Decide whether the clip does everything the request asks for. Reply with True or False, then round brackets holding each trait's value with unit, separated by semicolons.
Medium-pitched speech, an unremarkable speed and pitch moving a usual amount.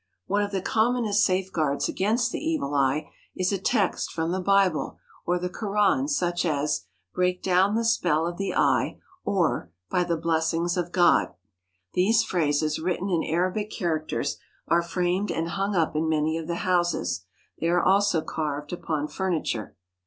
True (175 Hz; 165 wpm; 3.5 semitones)